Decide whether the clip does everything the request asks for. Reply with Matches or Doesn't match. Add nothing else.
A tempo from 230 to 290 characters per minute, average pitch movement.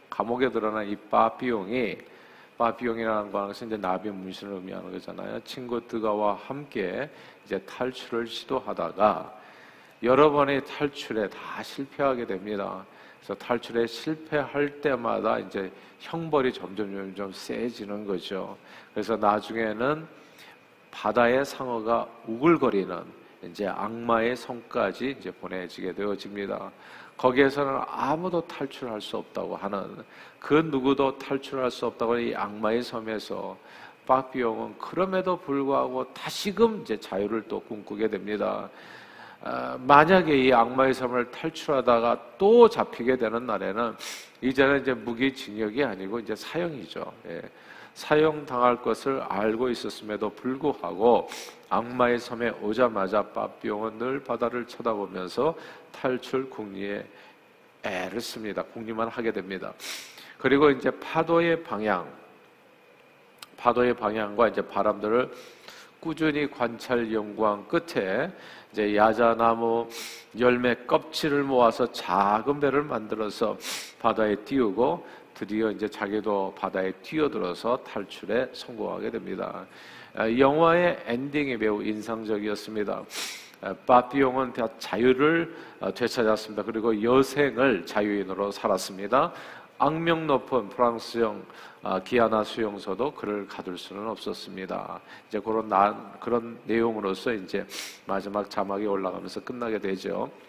Matches